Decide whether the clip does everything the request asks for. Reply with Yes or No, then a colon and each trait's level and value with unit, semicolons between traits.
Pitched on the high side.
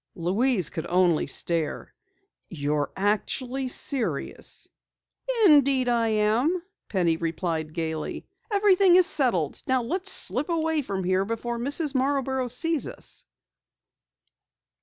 Yes: high, 240 Hz